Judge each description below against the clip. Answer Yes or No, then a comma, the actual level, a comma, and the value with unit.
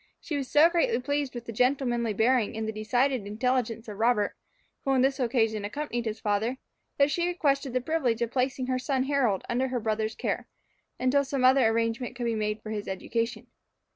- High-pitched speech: Yes, high, 245 Hz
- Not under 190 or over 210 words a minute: Yes, average, 200 wpm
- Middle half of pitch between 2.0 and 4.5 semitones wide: Yes, average, 3.4 semitones